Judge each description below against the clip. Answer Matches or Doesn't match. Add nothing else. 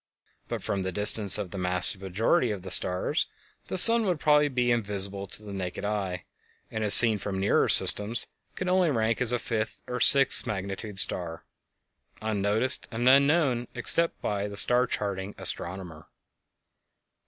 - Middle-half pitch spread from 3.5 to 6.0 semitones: Matches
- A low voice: Matches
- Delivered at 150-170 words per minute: Matches